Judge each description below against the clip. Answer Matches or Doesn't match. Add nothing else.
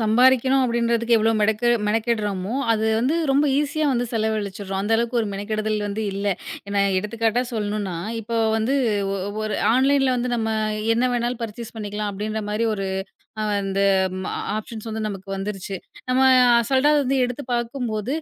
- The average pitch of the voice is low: Doesn't match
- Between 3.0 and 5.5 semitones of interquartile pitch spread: Doesn't match